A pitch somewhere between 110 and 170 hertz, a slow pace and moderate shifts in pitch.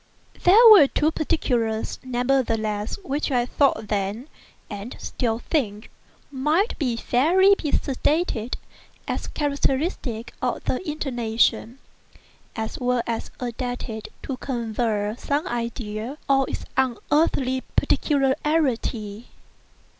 No: very high, 250 Hz; slow, 95 wpm; average, 4.2 semitones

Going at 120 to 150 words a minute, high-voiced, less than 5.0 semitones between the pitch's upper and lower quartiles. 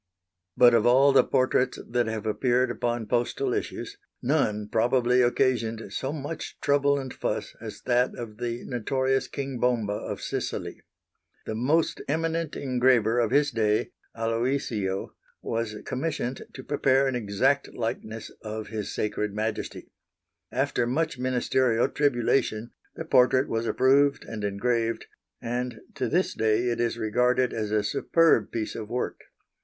No: average, 140 wpm; low, 120 Hz; average, 3.0 semitones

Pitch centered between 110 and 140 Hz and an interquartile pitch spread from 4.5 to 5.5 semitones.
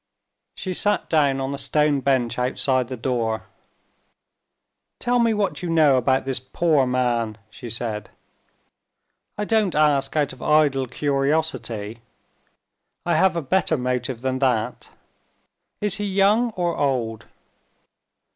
Yes: low, 135 Hz; average, 5.0 semitones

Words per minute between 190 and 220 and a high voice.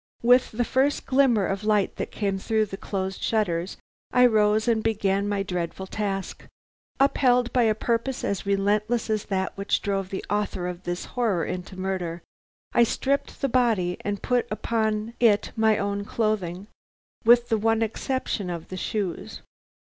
No: average, 165 wpm; high, 210 Hz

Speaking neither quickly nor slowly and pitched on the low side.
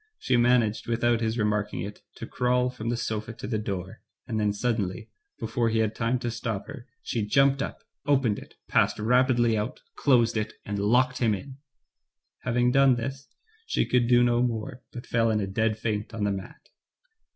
Yes: average, 190 wpm; low, 115 Hz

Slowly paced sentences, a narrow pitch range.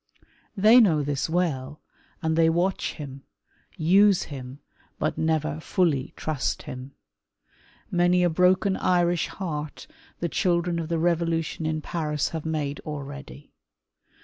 No: slow, 125 wpm; average, 3.1 semitones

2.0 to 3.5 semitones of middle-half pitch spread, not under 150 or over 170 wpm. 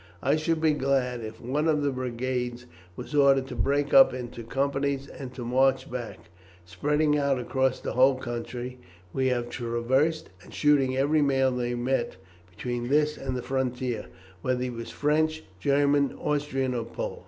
Yes: narrow, 2.6 semitones; average, 165 wpm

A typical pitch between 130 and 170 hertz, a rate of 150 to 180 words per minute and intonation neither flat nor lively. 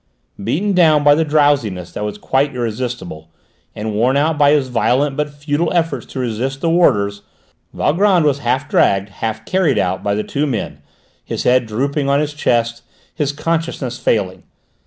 Yes: low, 135 Hz; average, 170 wpm; average, 5.0 semitones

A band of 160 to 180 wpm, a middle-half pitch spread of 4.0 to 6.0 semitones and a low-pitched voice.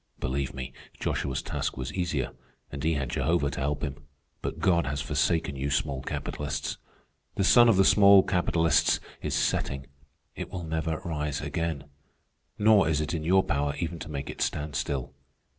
No: average, 175 wpm; average, 3.5 semitones; very low, 75 Hz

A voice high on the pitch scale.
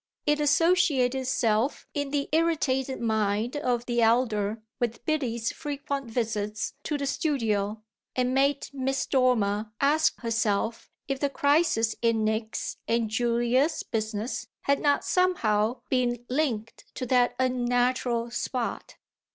Yes: high, 245 Hz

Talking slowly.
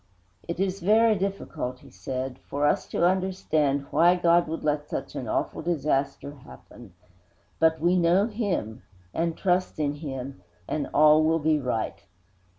No: average, 150 wpm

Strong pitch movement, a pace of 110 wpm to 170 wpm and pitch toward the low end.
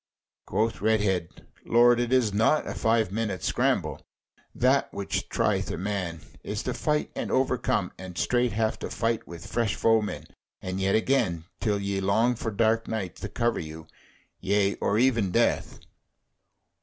No: average, 3.4 semitones; average, 155 wpm; low, 110 Hz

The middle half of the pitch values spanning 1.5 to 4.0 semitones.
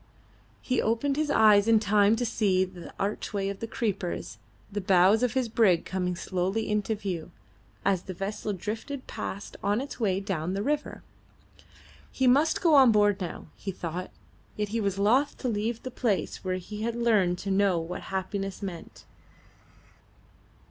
Yes: average, 3.3 semitones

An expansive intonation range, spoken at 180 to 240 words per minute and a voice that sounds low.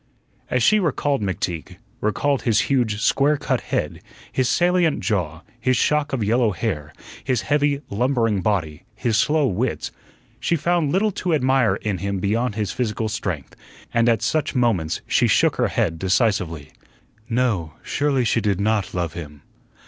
No: wide, 6.0 semitones; average, 155 wpm; low, 115 Hz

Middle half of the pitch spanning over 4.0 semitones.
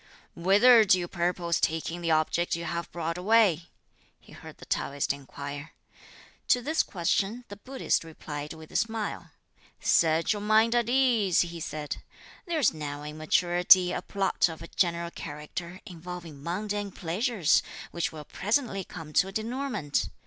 Yes: average, 4.7 semitones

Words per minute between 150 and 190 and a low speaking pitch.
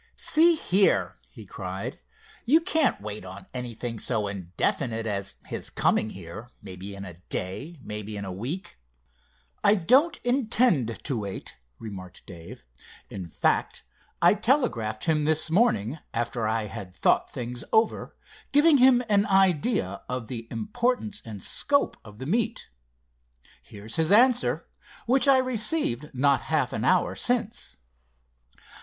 No: slow, 135 wpm; low, 130 Hz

